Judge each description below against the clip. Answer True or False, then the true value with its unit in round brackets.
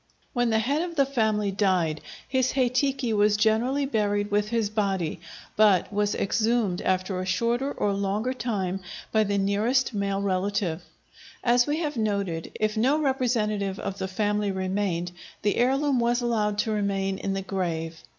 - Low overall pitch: False (210 Hz)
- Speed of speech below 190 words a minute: True (165 wpm)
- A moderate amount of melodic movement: True (3.6 semitones)